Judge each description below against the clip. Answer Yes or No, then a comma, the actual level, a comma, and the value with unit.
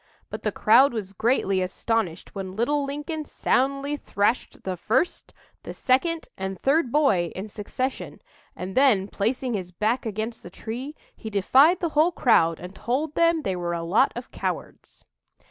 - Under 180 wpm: Yes, average, 165 wpm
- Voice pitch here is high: Yes, high, 235 Hz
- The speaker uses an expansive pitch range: Yes, wide, 6.5 semitones